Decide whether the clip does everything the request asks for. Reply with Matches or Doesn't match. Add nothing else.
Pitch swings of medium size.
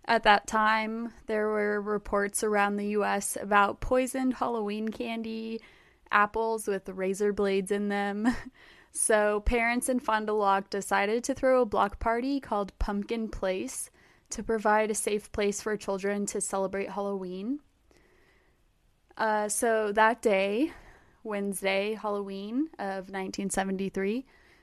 Doesn't match